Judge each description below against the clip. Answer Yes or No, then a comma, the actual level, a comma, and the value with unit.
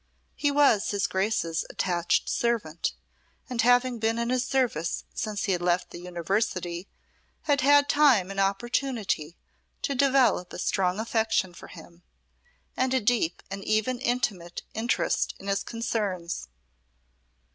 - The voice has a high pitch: Yes, high, 215 Hz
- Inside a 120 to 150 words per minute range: Yes, slow, 135 wpm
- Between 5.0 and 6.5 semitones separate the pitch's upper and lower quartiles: Yes, wide, 5.4 semitones